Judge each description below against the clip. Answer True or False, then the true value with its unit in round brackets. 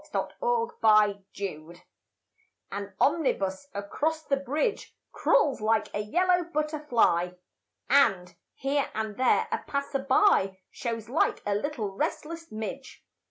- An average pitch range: False (7.0 semitones)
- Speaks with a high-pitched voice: True (260 Hz)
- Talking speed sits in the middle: False (115 wpm)